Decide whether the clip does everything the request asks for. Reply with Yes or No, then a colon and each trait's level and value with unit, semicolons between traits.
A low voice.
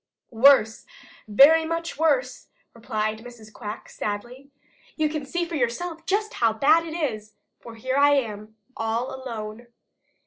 No: very high, 255 Hz